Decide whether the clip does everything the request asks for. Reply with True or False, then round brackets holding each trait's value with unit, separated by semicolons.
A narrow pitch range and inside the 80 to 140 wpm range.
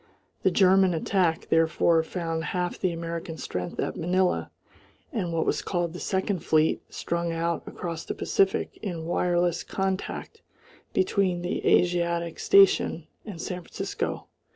True (2.0 semitones; 135 wpm)